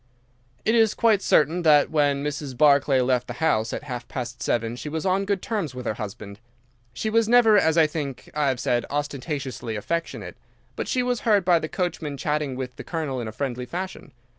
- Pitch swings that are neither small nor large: No, wide, 5.8 semitones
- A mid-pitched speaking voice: Yes, medium, 145 Hz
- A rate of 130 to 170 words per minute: No, fast, 205 wpm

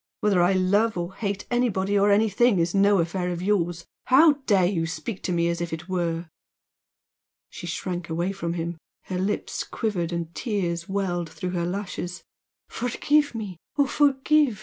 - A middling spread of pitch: Yes, average, 3.4 semitones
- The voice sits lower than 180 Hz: No, medium, 185 Hz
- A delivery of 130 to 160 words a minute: No, average, 170 wpm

